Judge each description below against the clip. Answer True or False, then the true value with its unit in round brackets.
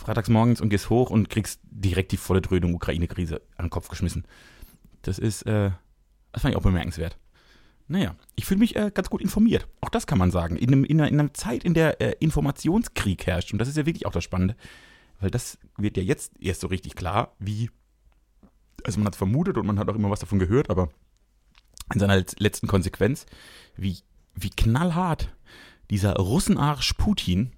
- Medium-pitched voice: False (100 Hz)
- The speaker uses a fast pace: True (200 wpm)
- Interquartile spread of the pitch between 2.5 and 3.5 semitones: False (5.1 semitones)